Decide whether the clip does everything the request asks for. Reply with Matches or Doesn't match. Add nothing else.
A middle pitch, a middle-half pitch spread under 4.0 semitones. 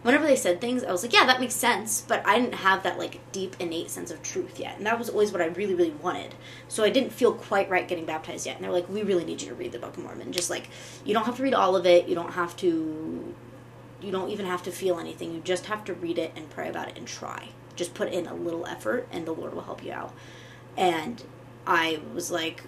Matches